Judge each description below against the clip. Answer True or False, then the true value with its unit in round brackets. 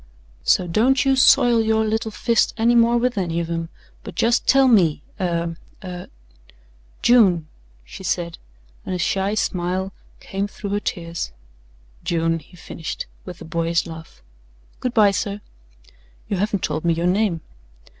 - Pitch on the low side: False (185 Hz)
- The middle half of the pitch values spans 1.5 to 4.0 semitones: False (4.9 semitones)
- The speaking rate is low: False (155 wpm)